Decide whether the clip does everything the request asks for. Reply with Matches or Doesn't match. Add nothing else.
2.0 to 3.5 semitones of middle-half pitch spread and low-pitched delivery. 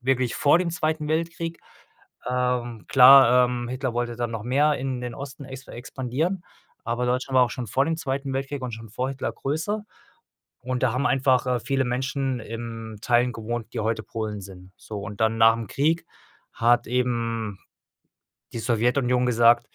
Matches